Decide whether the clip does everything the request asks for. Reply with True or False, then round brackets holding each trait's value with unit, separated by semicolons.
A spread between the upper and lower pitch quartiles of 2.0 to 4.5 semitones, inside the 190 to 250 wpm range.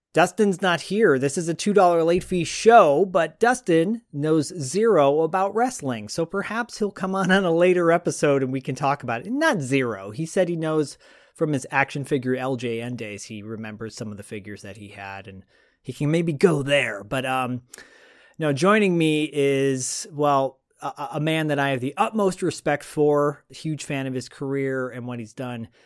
False (5.0 semitones; 200 wpm)